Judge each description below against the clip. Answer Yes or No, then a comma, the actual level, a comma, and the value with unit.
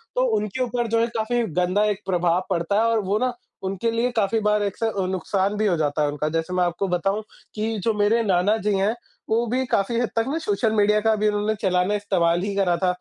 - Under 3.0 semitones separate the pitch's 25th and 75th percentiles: No, average, 3.3 semitones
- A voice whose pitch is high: Yes, high, 205 Hz